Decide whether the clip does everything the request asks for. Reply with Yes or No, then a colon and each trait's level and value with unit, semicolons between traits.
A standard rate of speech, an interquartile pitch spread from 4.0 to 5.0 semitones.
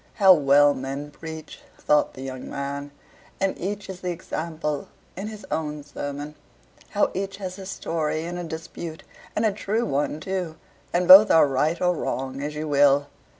Yes: average, 175 wpm; average, 4.4 semitones